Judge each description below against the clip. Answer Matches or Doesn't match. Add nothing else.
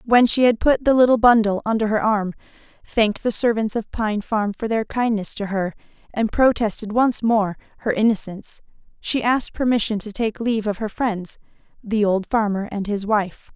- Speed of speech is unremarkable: Matches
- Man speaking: Doesn't match